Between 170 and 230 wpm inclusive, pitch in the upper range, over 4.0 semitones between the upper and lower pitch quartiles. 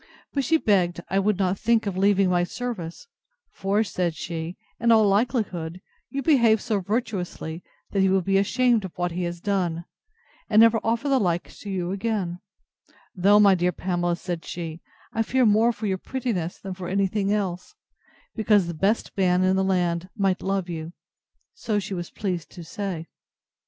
No: average, 180 wpm; high, 195 Hz; average, 3.4 semitones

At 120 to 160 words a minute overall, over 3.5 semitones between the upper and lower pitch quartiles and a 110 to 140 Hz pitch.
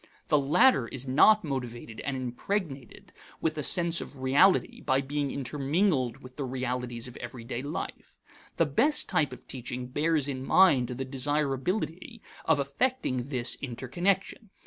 Yes: average, 145 wpm; average, 4.1 semitones; low, 135 Hz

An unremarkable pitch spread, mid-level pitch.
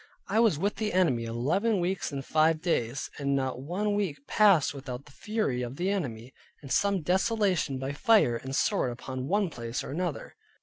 No: wide, 7.0 semitones; medium, 155 Hz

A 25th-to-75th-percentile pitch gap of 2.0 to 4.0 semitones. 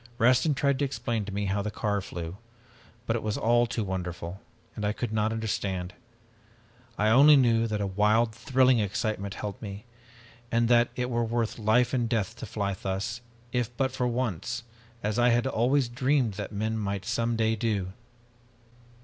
Yes: average, 2.9 semitones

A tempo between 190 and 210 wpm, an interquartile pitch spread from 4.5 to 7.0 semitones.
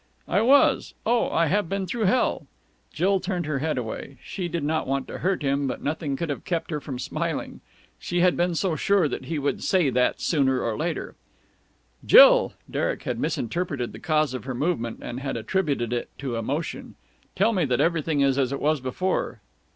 Yes: average, 195 wpm; average, 5.0 semitones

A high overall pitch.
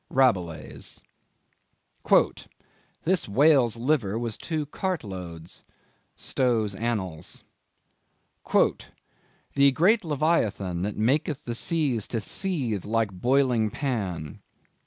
No: low, 115 Hz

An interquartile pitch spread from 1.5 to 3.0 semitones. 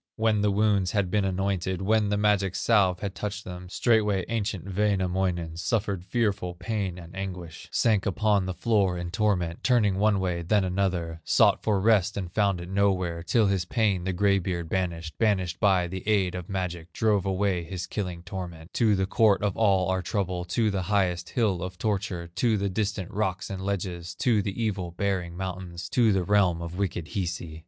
Yes: narrow, 2.6 semitones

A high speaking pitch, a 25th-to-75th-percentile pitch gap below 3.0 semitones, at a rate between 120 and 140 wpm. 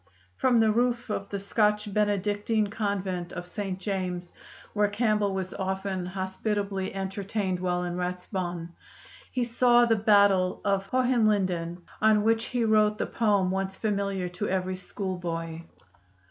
Yes: high, 200 Hz; narrow, 2.5 semitones; slow, 135 wpm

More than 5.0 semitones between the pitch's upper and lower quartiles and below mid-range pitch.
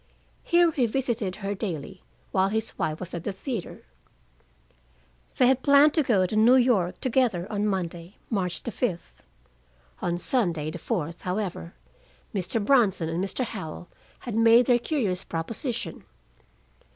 No: wide, 5.4 semitones; high, 205 Hz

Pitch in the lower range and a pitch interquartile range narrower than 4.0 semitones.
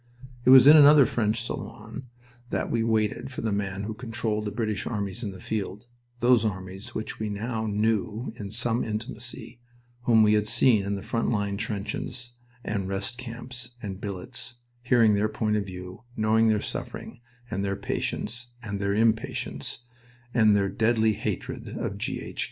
Yes: low, 110 Hz; narrow, 2.4 semitones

